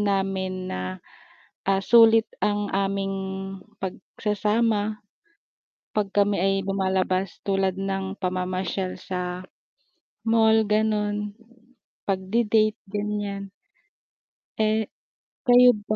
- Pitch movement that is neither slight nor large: No, narrow, 2.0 semitones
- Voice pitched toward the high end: Yes, high, 200 Hz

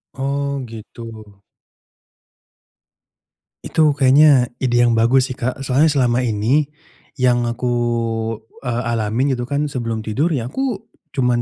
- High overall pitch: No, low, 130 Hz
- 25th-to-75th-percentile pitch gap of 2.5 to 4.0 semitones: Yes, average, 2.9 semitones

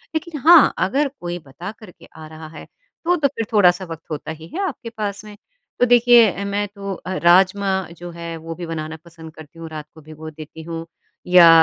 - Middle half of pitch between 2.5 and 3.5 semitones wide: No, average, 5.1 semitones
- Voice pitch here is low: No, medium, 180 Hz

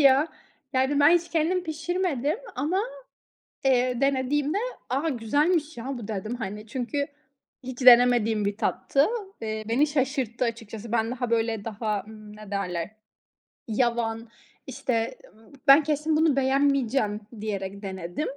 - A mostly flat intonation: No, average, 4.6 semitones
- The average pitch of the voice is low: No, high, 245 Hz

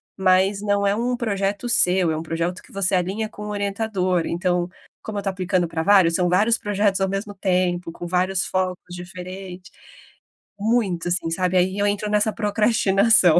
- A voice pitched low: No, high, 190 Hz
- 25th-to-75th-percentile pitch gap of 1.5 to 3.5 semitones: Yes, narrow, 2.4 semitones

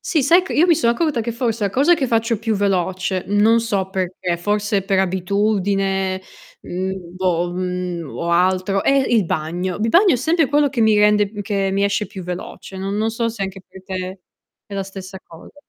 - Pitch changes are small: No, average, 3.4 semitones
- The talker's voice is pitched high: Yes, high, 195 Hz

